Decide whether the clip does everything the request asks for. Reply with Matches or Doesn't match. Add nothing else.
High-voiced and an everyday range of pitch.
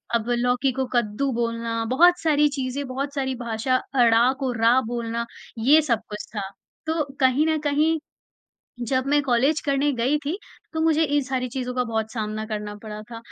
Matches